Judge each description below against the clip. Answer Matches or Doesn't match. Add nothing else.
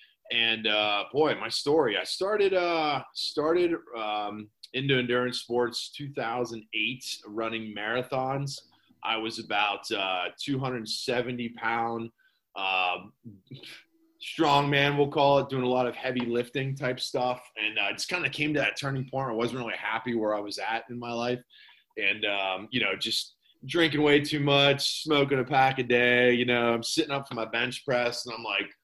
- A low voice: Matches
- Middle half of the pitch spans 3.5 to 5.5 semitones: Matches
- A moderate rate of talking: Matches